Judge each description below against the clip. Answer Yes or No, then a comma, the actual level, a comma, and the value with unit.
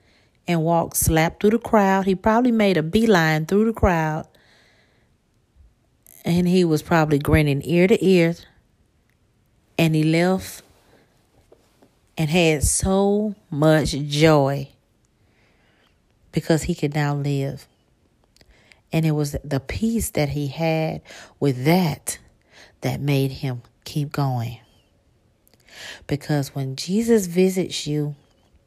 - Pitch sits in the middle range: Yes, medium, 155 Hz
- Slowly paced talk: Yes, slow, 115 wpm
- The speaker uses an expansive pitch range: No, average, 4.2 semitones